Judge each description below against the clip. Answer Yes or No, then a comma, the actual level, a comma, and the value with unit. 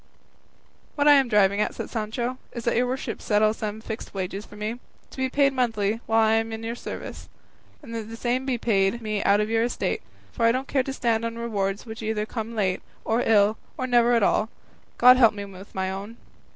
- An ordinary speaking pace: No, fast, 225 wpm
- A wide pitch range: No, narrow, 2.4 semitones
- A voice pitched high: Yes, high, 225 Hz